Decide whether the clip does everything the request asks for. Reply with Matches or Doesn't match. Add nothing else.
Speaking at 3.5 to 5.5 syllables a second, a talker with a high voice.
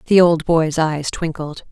Doesn't match